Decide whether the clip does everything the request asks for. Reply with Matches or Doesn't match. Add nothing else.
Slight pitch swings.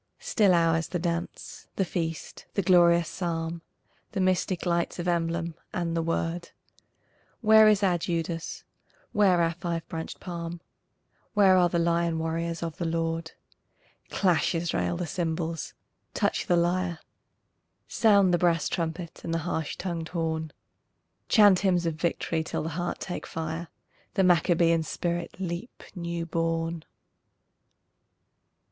Matches